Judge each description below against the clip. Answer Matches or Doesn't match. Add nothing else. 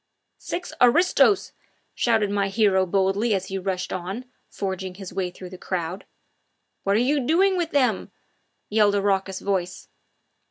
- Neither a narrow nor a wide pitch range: Matches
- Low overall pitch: Doesn't match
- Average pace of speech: Matches